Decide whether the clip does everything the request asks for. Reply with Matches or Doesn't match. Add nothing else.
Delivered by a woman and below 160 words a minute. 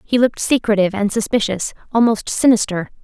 Matches